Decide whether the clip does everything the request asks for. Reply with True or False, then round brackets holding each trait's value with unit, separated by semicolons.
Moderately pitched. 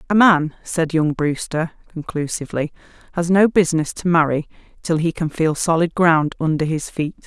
True (165 Hz)